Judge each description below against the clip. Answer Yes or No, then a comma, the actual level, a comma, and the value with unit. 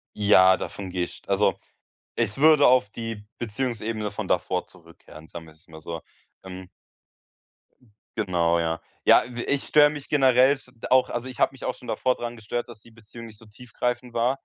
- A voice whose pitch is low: Yes, low, 115 Hz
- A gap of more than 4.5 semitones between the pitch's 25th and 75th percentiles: Yes, average, 5.2 semitones